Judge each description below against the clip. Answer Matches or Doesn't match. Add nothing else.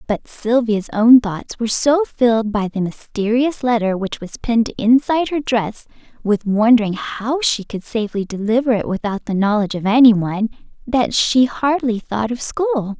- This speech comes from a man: Doesn't match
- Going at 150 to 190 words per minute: Matches